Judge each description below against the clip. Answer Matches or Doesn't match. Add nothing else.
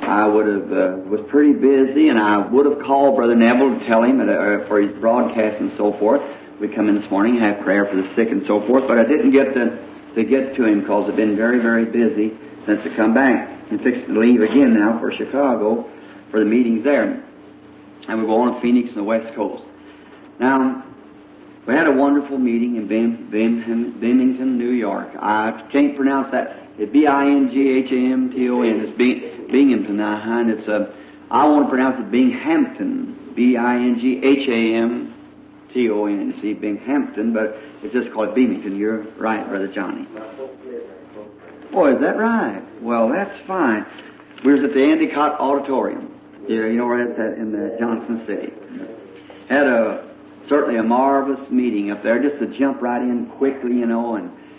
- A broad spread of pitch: Doesn't match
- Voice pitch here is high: Doesn't match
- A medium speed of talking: Matches